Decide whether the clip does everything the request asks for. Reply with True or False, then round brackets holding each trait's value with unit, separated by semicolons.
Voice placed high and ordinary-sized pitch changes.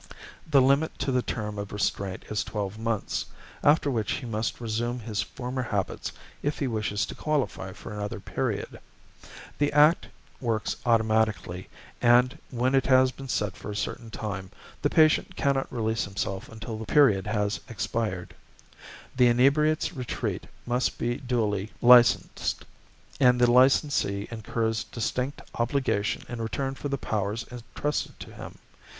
False (120 Hz; 3.7 semitones)